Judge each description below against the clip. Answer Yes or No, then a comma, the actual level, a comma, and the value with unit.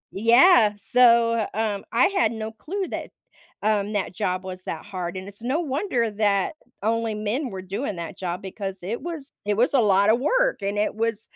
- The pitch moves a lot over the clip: No, average, 3.5 semitones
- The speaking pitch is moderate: No, high, 215 Hz